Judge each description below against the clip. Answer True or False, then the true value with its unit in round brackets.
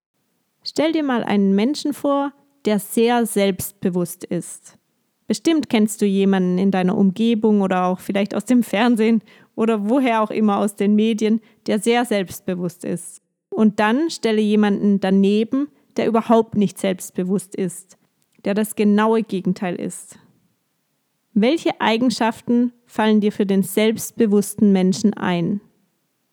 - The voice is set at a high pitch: True (210 Hz)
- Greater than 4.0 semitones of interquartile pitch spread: False (2.7 semitones)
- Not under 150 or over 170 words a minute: False (130 wpm)